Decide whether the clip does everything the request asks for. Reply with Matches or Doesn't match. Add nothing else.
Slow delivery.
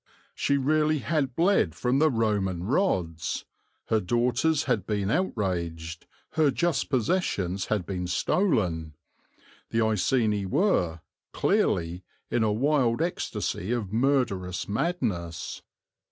Matches